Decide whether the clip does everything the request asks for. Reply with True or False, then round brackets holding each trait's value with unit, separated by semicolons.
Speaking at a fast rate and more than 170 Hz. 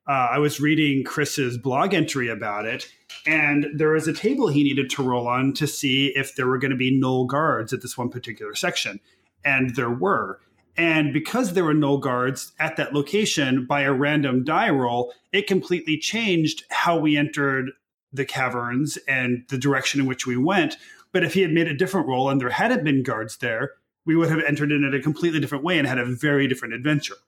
False (210 wpm; 140 Hz)